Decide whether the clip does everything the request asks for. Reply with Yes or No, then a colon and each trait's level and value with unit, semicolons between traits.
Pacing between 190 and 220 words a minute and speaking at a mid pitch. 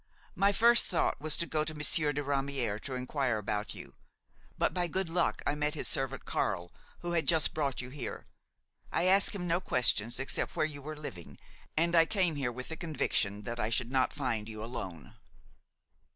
Yes: average, 195 wpm; medium, 145 Hz